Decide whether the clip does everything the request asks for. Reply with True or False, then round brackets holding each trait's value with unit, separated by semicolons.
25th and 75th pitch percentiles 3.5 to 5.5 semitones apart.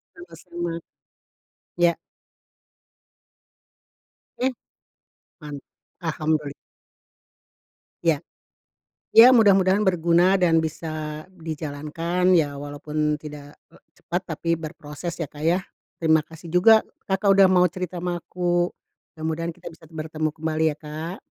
False (2.5 semitones)